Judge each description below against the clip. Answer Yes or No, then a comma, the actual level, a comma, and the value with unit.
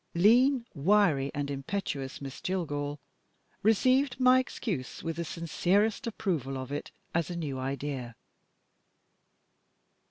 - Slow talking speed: Yes, slow, 115 wpm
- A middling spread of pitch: No, wide, 7.1 semitones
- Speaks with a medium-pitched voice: Yes, medium, 170 Hz